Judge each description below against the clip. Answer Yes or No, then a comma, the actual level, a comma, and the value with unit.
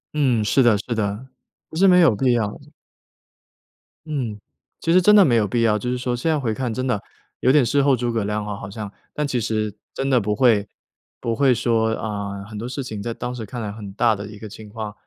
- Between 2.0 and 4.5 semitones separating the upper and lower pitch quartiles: Yes, average, 3.4 semitones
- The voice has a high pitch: No, low, 115 Hz